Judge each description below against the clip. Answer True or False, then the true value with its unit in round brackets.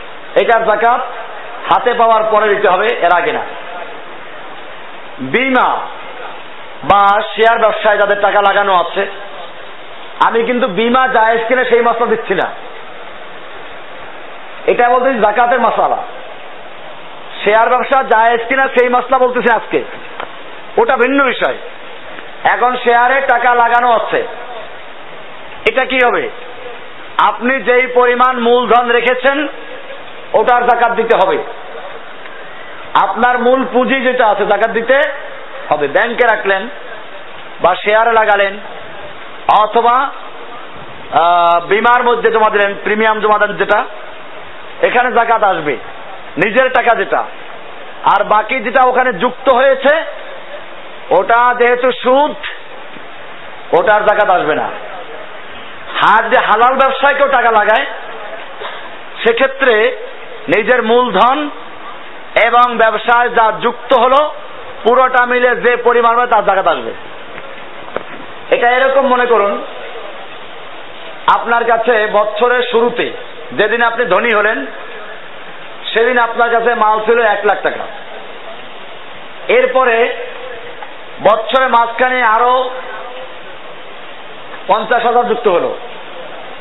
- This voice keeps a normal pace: True (105 wpm)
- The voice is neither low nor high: False (240 Hz)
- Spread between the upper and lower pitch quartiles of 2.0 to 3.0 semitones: True (2.6 semitones)